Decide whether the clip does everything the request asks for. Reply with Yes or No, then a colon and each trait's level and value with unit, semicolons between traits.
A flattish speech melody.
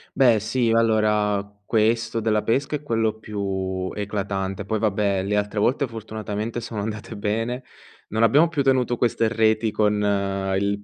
Yes: narrow, 2.0 semitones